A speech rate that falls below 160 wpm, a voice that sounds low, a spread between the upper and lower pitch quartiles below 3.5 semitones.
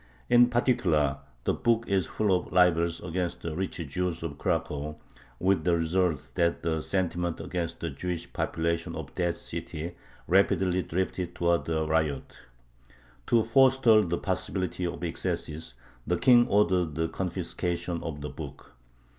Yes: average, 145 wpm; very low, 85 Hz; narrow, 2.4 semitones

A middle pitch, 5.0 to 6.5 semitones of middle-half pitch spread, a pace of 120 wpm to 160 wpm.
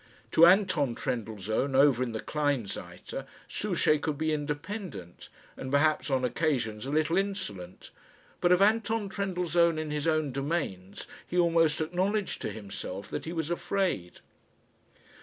Yes: medium, 155 Hz; wide, 5.6 semitones; average, 140 wpm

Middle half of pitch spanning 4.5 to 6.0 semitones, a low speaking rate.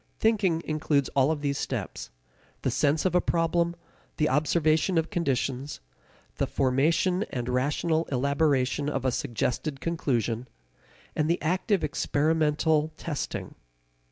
No: average, 3.3 semitones; slow, 125 wpm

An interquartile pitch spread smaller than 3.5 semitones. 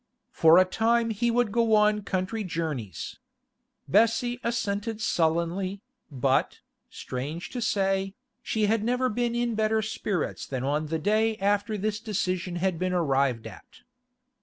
No: average, 4.8 semitones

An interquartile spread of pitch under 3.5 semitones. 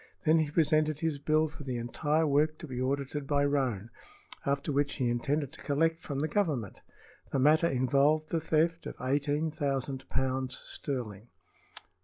Yes: average, 2.7 semitones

